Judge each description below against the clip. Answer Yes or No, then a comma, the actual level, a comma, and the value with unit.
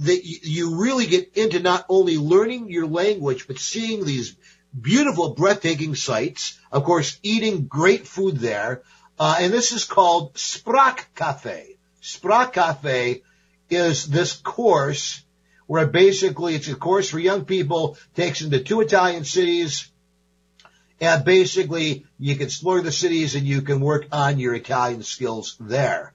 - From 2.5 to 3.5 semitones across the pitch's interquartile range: No, average, 5.1 semitones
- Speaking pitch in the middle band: Yes, medium, 165 Hz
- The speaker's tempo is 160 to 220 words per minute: No, average, 145 wpm